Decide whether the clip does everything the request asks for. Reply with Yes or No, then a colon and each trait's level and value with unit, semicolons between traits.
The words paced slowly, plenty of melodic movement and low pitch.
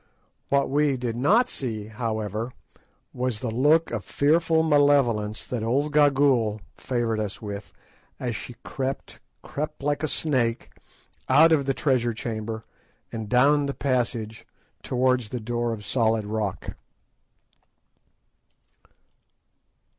No: slow, 120 wpm; average, 4.2 semitones; low, 125 Hz